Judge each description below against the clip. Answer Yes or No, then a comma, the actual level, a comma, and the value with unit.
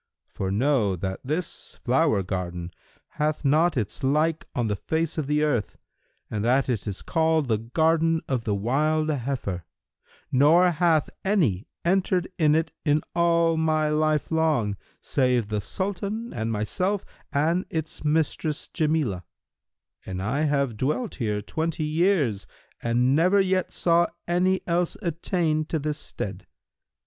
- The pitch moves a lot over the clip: Yes, wide, 5.9 semitones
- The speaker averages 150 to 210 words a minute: No, average, 140 wpm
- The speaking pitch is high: No, medium, 150 Hz